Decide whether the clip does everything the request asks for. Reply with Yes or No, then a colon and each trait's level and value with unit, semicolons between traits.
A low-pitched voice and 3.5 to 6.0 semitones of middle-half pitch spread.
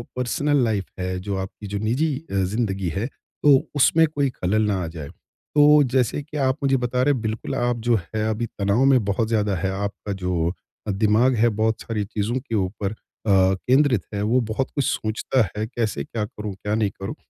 Yes: low, 110 Hz; average, 4.2 semitones